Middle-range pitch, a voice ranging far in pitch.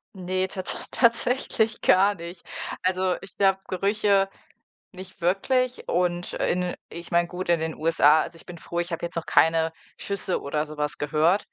No: medium, 180 Hz; average, 2.7 semitones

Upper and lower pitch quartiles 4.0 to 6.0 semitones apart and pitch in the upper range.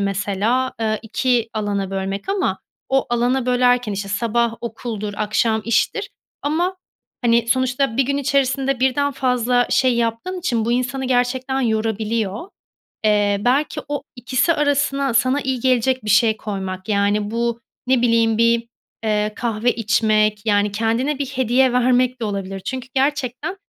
No: average, 3.4 semitones; high, 235 Hz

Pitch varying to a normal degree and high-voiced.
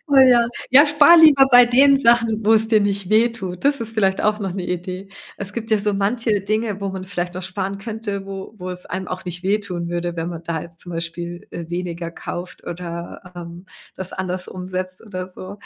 Yes: average, 3.7 semitones; high, 195 Hz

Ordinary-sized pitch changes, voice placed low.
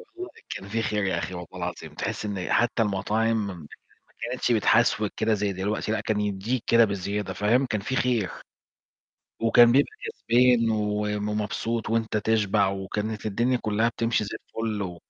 No: narrow, 2.3 semitones; low, 105 Hz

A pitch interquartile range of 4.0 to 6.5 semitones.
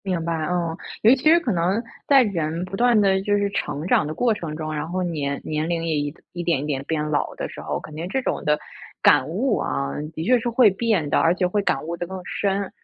Yes: average, 4.7 semitones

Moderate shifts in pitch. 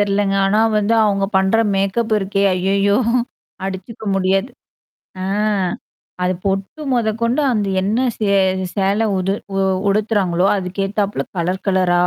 No: narrow, 1.8 semitones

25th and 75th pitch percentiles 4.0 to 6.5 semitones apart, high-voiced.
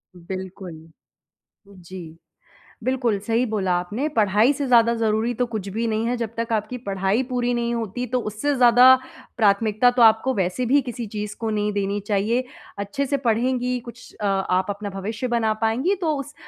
No: average, 3.4 semitones; high, 225 Hz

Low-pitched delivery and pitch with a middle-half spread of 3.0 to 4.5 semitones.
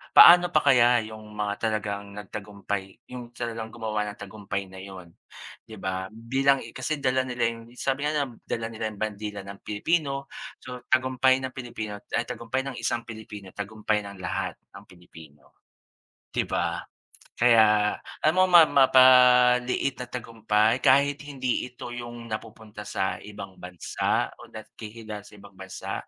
Yes: low, 115 Hz; average, 3.6 semitones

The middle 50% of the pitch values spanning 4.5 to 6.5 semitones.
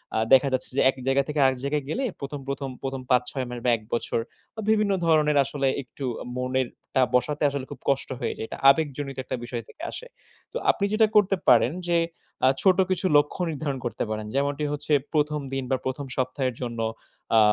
No: average, 2.8 semitones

